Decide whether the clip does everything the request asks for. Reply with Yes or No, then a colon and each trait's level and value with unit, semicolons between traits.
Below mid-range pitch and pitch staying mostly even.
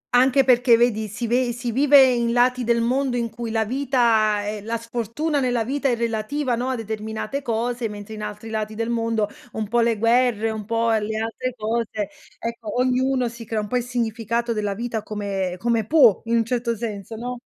No: high, 230 Hz; narrow, 2.1 semitones